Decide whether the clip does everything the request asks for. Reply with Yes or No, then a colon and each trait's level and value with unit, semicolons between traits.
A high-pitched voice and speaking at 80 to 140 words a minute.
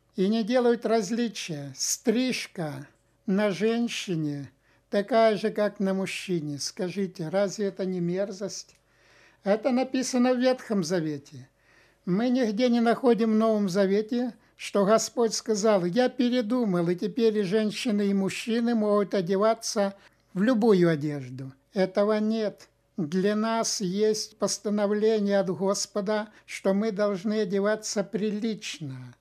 Yes: high, 205 Hz; average, 120 wpm